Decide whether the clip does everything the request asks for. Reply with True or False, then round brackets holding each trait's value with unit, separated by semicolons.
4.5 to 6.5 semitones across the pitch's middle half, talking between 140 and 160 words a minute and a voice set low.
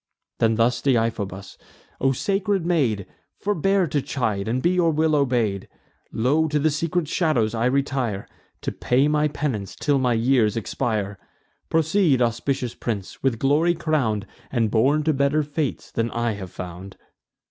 True (5.2 semitones; 150 wpm; 130 Hz)